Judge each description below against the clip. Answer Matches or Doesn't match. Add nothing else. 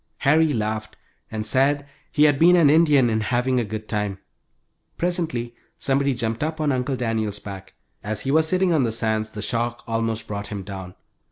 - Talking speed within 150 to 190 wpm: Matches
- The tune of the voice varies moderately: Matches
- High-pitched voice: Doesn't match